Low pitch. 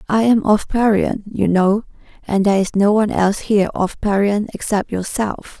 No: high, 205 Hz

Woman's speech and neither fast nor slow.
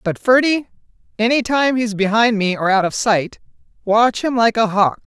Yes: female; average, 185 wpm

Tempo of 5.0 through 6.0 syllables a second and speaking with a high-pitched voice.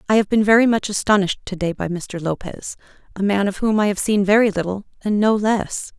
Yes: 5.8 syllables/s; high, 200 Hz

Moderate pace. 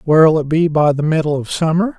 No: fast, 240 wpm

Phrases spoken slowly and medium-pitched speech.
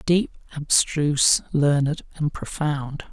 Yes: slow, 95 wpm; medium, 150 Hz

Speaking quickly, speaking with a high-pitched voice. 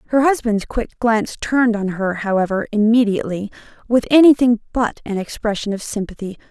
No: average, 150 wpm; high, 220 Hz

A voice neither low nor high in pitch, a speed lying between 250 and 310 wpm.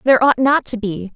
No: high, 240 Hz; fast, 260 wpm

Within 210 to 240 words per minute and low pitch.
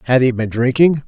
Yes: fast, 225 wpm; low, 130 Hz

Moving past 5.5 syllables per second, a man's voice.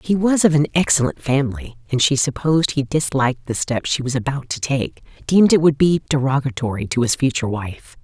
No: 5.8 syllables/s; female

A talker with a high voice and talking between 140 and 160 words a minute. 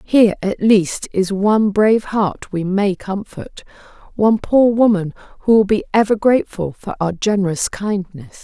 Yes: high, 200 Hz; average, 155 wpm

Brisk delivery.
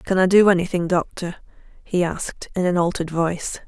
No: average, 180 wpm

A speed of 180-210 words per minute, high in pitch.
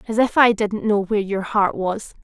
No: fast, 240 wpm; high, 210 Hz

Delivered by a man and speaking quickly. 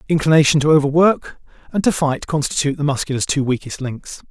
No: male; average, 165 wpm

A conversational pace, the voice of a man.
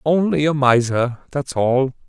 Yes: average, 145 wpm; male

